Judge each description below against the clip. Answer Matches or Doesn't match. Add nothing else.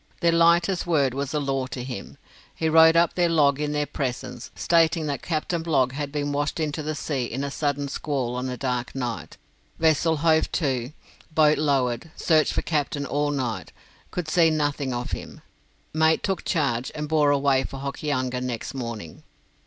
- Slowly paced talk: Doesn't match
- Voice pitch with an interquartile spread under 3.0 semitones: Doesn't match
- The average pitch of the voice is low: Doesn't match